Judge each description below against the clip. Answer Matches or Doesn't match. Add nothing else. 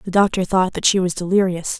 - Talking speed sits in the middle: Doesn't match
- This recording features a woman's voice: Matches